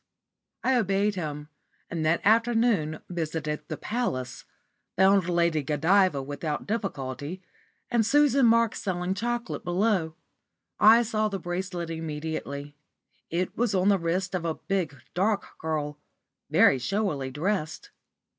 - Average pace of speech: No, slow, 125 wpm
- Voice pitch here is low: No, medium, 180 Hz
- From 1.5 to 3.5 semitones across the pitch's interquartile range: No, average, 5.2 semitones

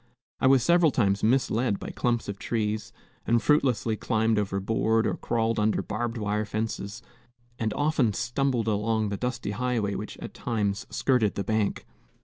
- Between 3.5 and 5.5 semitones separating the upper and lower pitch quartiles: No, narrow, 2.5 semitones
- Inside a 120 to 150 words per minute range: No, average, 160 wpm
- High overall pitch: No, low, 110 Hz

